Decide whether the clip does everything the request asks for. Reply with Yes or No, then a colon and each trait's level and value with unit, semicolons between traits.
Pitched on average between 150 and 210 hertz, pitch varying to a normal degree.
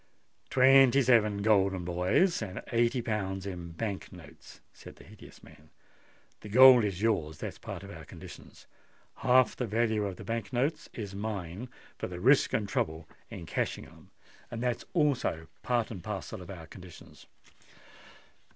No: low, 105 Hz; average, 4.8 semitones